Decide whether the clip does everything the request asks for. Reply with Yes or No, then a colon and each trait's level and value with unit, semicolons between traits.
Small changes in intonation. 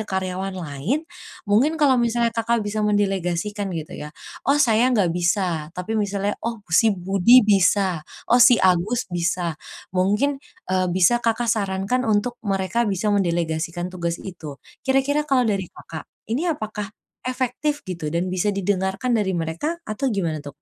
No: average, 4.8 semitones